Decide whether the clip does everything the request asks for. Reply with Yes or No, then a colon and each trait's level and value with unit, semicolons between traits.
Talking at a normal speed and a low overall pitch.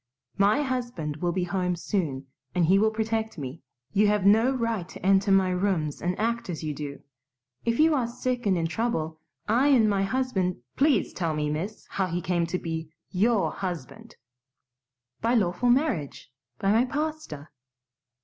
No: average, 170 wpm; high, 195 Hz